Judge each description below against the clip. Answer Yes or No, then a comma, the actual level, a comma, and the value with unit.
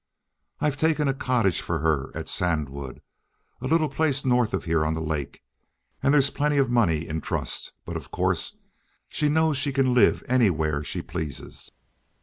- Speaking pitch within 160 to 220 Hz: No, low, 120 Hz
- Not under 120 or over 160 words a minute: No, average, 170 wpm